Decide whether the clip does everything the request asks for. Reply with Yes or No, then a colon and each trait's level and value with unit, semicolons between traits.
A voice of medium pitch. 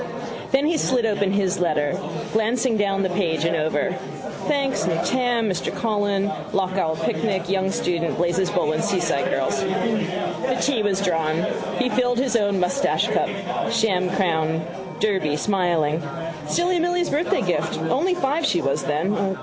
No: high, 195 Hz